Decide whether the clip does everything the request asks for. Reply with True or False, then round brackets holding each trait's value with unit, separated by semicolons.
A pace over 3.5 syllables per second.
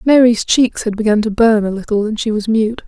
True (5.5 syllables/s)